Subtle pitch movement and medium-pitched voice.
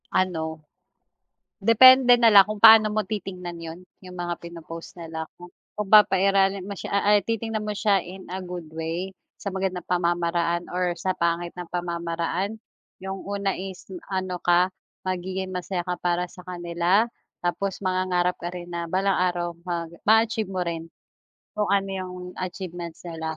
Yes: narrow, 2.2 semitones; medium, 180 Hz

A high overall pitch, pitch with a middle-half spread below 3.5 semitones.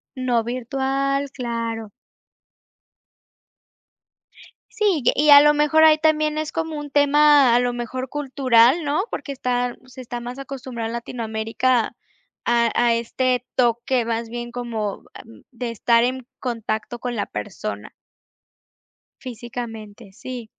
Yes: high, 245 Hz; average, 2.9 semitones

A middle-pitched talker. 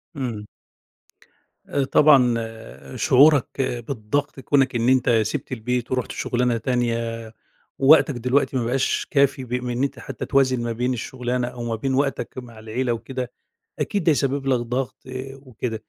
No: low, 125 Hz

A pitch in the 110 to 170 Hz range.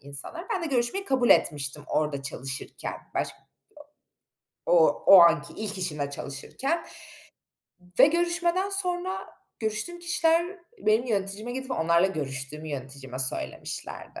No: high, 215 Hz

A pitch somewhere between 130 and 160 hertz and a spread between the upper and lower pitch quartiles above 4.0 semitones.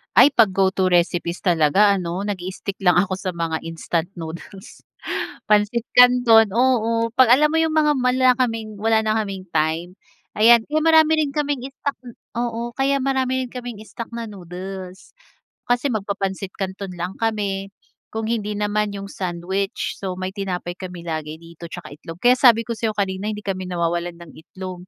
No: high, 200 Hz; average, 4.6 semitones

